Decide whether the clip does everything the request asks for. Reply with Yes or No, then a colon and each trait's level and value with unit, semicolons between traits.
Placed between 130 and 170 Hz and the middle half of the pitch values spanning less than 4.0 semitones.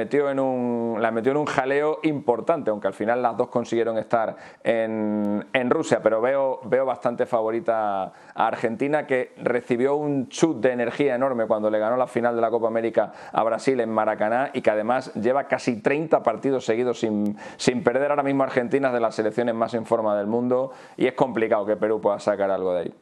No: low, 120 Hz; average, 3.3 semitones